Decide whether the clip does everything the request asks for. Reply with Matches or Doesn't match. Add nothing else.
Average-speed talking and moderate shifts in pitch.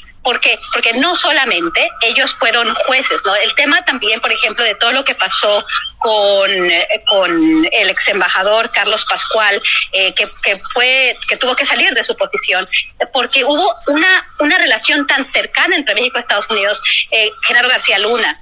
Doesn't match